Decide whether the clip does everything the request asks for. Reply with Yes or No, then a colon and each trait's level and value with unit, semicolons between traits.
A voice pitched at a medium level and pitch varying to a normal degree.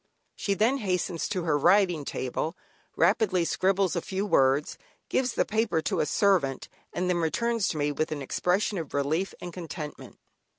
Yes: medium, 180 Hz; average, 4.4 semitones